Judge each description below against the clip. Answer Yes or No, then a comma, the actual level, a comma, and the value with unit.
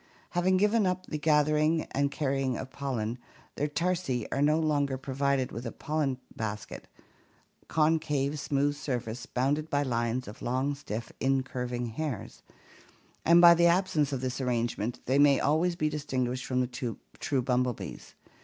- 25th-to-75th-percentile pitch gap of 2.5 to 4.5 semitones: Yes, average, 3.4 semitones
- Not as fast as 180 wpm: Yes, average, 150 wpm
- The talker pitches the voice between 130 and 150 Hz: Yes, medium, 140 Hz